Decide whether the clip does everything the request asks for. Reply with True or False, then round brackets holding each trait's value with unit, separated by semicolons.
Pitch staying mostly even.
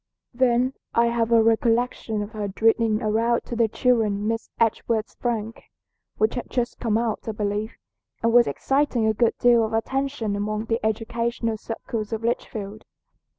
True (1.6 semitones)